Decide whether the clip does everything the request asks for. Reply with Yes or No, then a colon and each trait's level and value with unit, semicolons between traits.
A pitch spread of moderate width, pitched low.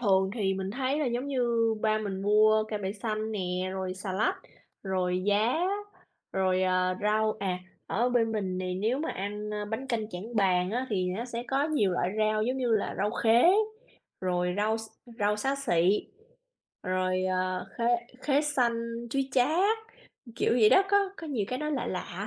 No: average, 4.3 semitones; high, 215 Hz